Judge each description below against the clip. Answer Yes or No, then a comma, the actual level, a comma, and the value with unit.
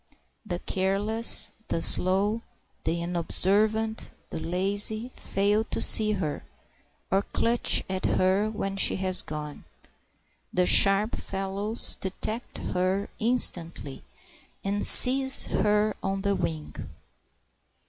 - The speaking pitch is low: No, high, 195 Hz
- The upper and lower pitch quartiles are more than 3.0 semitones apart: No, average, 2.7 semitones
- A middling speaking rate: No, slow, 105 wpm